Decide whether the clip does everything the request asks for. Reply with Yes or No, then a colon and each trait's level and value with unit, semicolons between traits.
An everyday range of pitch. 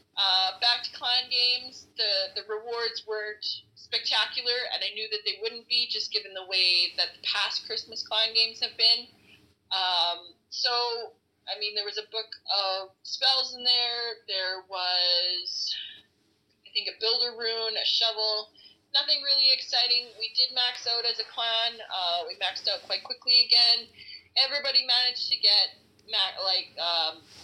Yes: average, 4.4 semitones